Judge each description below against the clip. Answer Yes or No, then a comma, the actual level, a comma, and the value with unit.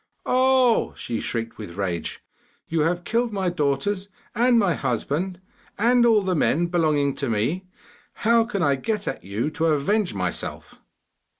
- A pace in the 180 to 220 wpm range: No, average, 155 wpm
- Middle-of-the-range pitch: Yes, medium, 175 Hz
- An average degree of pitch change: No, wide, 7.6 semitones